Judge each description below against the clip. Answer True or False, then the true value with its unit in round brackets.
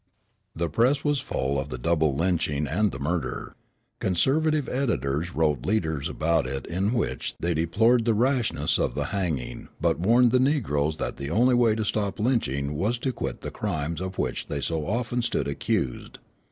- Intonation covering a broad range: True (8.1 semitones)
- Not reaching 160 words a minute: False (180 wpm)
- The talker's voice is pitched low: True (90 Hz)